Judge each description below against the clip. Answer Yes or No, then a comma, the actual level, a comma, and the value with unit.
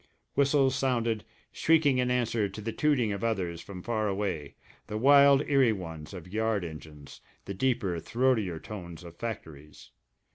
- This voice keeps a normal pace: Yes, average, 150 wpm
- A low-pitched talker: Yes, low, 110 Hz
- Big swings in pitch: Yes, wide, 6.1 semitones